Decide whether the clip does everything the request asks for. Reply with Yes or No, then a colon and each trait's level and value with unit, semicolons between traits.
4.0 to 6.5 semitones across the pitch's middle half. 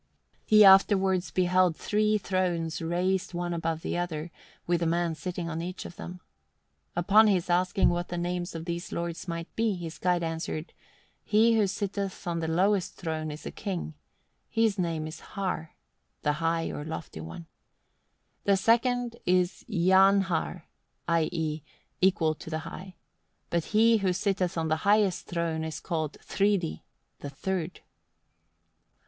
No: average, 2.8 semitones